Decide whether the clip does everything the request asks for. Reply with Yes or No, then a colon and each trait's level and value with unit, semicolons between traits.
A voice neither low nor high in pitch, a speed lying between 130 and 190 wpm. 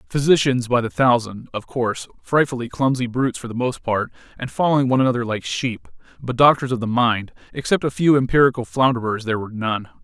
No: low, 125 Hz; average, 180 wpm